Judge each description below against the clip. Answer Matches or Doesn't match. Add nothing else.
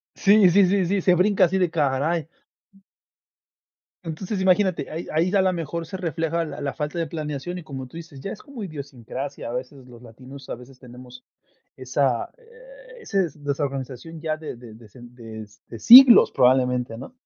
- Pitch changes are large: Matches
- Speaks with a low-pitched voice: Doesn't match